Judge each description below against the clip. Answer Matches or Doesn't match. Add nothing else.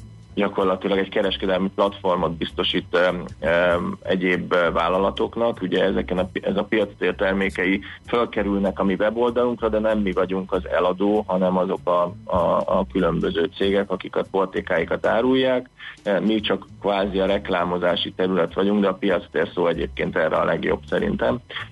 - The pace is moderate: Matches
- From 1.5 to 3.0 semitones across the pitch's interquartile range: Matches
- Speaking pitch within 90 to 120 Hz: Matches